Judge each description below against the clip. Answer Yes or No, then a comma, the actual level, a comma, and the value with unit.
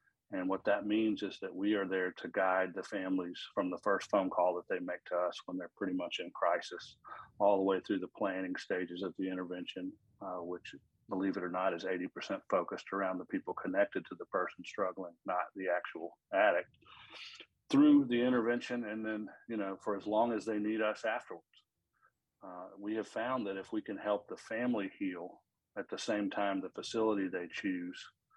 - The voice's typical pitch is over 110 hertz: No, low, 100 Hz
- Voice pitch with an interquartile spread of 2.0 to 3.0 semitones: Yes, average, 2.7 semitones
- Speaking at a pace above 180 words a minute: Yes, average, 200 wpm